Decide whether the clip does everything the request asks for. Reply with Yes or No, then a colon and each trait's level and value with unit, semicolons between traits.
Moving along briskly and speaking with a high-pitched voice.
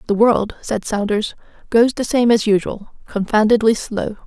No: average, 155 wpm; high, 220 Hz